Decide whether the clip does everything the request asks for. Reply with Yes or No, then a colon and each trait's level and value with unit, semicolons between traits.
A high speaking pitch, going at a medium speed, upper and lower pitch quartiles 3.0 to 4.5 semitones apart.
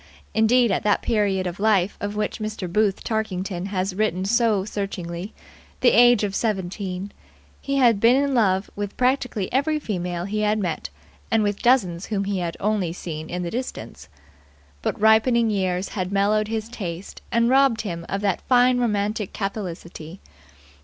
Yes: high, 205 Hz; average, 160 wpm; average, 3.3 semitones